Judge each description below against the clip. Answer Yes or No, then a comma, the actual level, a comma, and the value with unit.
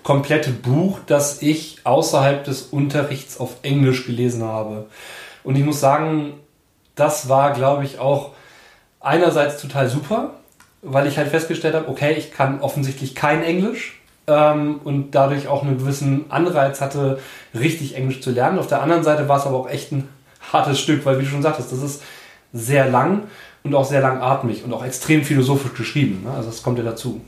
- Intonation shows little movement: Yes, narrow, 2.1 semitones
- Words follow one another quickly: No, average, 180 wpm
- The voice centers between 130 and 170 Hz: Yes, medium, 140 Hz